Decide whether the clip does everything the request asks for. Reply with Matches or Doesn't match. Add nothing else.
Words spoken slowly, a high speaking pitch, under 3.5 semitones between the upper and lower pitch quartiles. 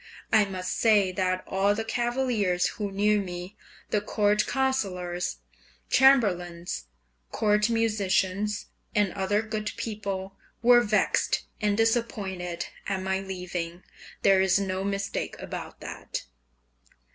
Matches